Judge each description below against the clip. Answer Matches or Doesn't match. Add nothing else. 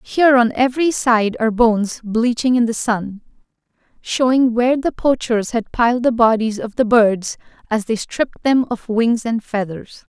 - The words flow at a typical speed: Matches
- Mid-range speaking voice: Doesn't match